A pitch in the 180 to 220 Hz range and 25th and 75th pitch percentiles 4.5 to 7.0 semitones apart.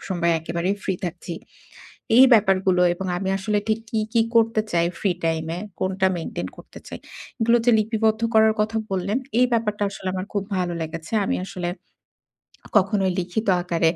No: high, 190 Hz; average, 3.7 semitones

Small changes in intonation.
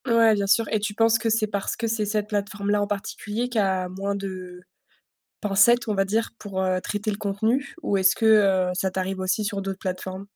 Yes: narrow, 2.3 semitones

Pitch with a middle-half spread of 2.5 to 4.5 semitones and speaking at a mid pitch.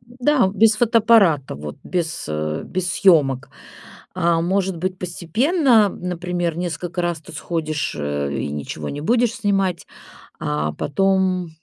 No: average, 5.0 semitones; medium, 175 Hz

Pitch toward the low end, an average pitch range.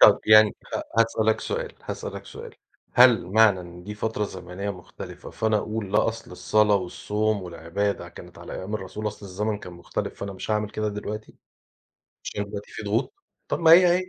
No: low, 105 Hz; narrow, 1.7 semitones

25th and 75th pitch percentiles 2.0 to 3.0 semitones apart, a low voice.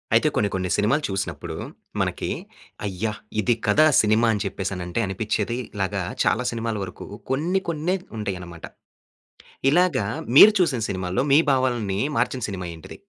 No: wide, 5.4 semitones; low, 105 Hz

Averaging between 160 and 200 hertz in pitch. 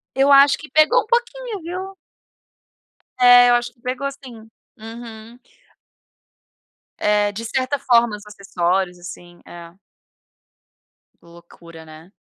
No: high, 235 Hz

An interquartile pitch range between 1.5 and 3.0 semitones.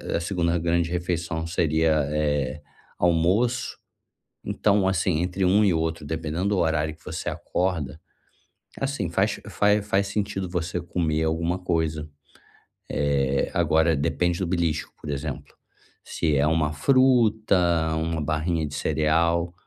Yes: average, 2.7 semitones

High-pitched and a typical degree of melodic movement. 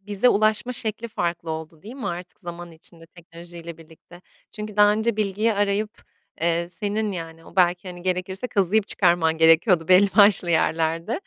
No: medium, 180 Hz; average, 3.8 semitones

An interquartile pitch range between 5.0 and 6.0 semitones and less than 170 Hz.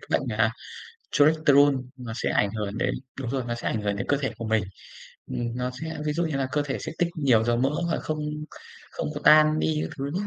No: average, 4.5 semitones; low, 135 Hz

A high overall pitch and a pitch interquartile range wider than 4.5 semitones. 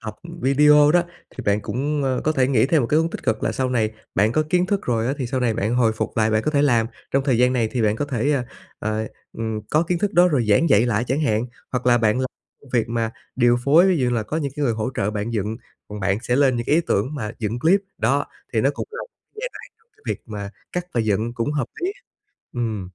No: low, 125 Hz; average, 4.9 semitones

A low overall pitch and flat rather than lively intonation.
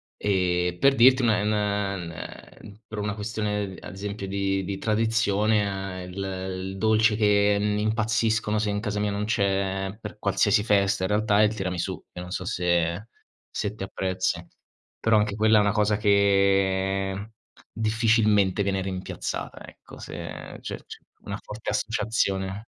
Yes: low, 100 Hz; narrow, 1.9 semitones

